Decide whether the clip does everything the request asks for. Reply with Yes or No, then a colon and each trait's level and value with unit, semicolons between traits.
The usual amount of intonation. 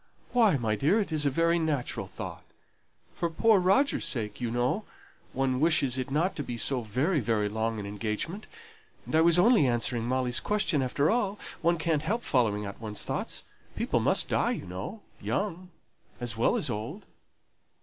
No: wide, 6.8 semitones